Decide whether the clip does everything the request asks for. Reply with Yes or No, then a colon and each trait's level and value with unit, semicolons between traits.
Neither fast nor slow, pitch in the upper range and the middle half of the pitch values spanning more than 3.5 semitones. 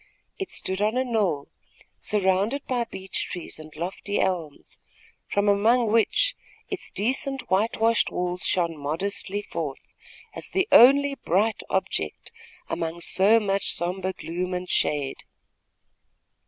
No: slow, 125 wpm; high, 195 Hz; average, 4.4 semitones